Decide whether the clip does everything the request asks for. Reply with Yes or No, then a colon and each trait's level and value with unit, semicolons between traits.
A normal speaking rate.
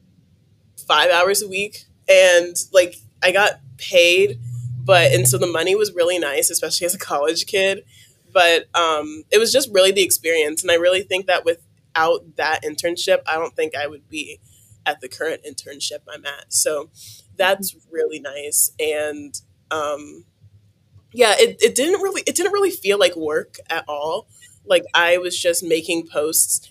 Yes: average, 170 wpm